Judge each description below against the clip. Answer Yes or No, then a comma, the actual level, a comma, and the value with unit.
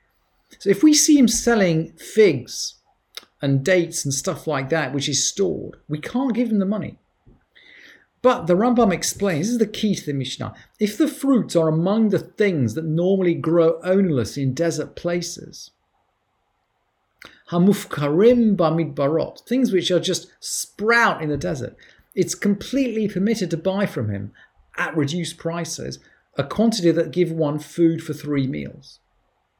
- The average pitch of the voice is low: No, medium, 175 Hz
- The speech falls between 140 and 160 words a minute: Yes, average, 150 wpm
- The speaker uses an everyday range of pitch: Yes, average, 4.9 semitones